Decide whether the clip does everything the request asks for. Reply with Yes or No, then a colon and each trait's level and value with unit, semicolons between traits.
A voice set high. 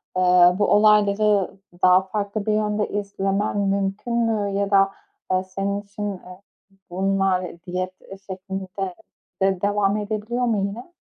Yes: high, 200 Hz